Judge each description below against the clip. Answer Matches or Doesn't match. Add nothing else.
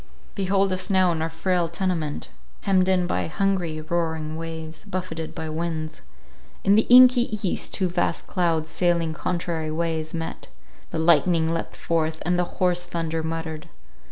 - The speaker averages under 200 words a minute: Matches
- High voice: Doesn't match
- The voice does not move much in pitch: Matches